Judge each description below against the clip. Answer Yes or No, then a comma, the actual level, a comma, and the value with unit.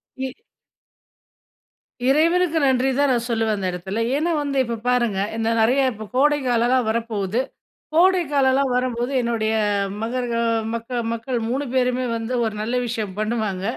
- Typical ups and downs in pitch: Yes, average, 3.1 semitones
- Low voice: No, high, 245 Hz